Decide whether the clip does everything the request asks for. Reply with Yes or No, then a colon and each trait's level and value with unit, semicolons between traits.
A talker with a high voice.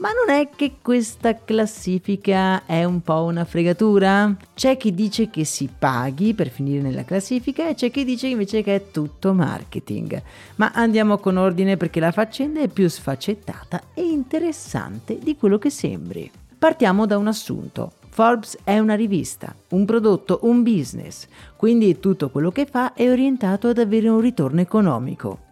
Yes: high, 210 Hz